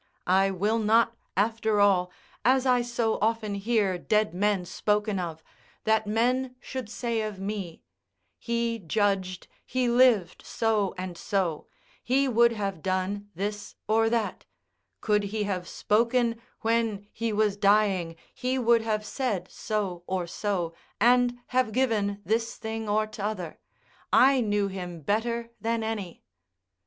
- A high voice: Yes, high, 215 Hz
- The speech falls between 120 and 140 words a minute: Yes, slow, 135 wpm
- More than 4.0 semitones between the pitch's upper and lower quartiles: No, average, 2.8 semitones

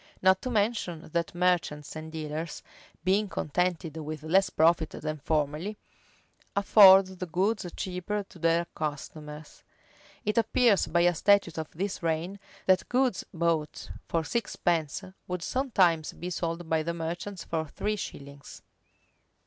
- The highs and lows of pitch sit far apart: No, average, 3.4 semitones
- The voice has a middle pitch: Yes, medium, 170 Hz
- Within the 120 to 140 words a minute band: Yes, slow, 135 wpm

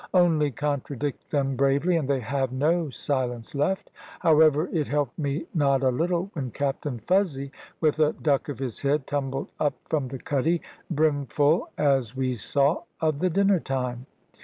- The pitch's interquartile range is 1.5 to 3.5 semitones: Yes, average, 2.7 semitones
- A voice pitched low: No, medium, 145 Hz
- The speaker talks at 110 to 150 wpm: No, average, 160 wpm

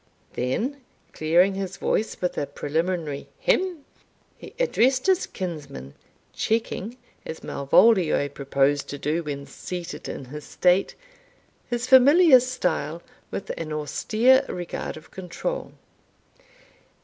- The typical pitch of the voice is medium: Yes, medium, 180 Hz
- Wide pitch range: Yes, wide, 8.6 semitones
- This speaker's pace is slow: Yes, slow, 115 wpm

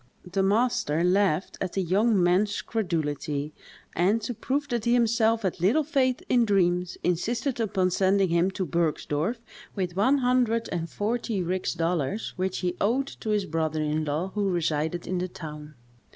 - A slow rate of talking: No, average, 165 wpm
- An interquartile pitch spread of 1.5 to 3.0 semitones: No, average, 4.9 semitones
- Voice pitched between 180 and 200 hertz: Yes, high, 190 Hz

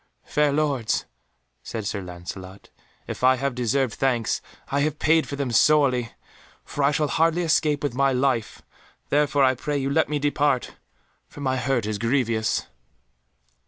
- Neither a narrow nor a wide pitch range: Yes, average, 3.6 semitones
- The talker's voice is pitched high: No, low, 135 Hz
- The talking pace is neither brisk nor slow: Yes, average, 160 wpm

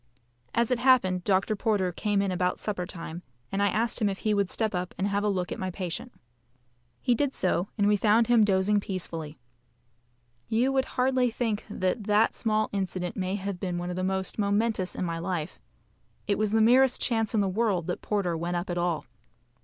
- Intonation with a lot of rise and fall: No, average, 3.3 semitones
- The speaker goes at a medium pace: No, fast, 210 wpm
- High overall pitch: Yes, high, 200 Hz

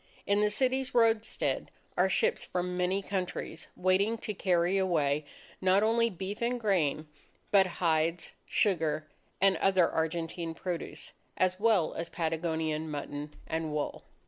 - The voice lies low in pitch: No, medium, 180 Hz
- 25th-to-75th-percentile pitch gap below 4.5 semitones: Yes, average, 3.8 semitones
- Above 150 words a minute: No, slow, 135 wpm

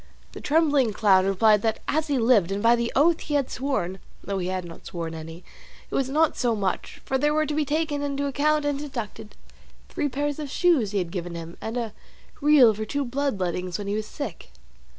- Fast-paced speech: Yes, fast, 220 wpm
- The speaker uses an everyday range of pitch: No, wide, 6.7 semitones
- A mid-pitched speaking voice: No, high, 240 Hz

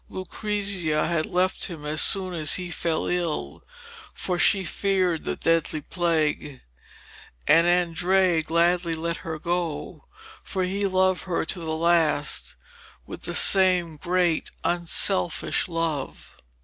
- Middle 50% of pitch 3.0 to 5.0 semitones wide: No, narrow, 2.4 semitones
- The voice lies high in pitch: No, medium, 170 Hz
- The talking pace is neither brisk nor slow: No, slow, 125 wpm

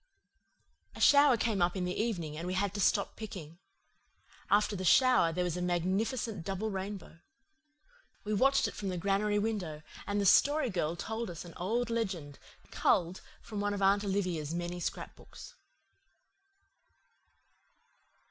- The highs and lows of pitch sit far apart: No, average, 3.5 semitones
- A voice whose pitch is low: No, high, 195 Hz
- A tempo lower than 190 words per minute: Yes, average, 150 wpm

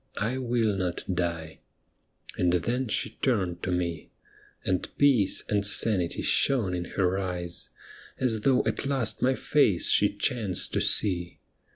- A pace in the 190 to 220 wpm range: No, average, 145 wpm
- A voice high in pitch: No, low, 100 Hz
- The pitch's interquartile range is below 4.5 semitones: No, average, 5.2 semitones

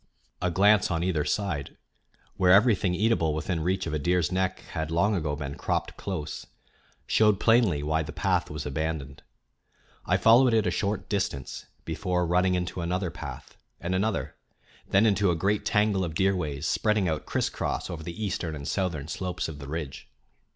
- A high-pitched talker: No, very low, 90 Hz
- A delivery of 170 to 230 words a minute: Yes, average, 175 wpm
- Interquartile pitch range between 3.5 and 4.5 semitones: Yes, average, 4.0 semitones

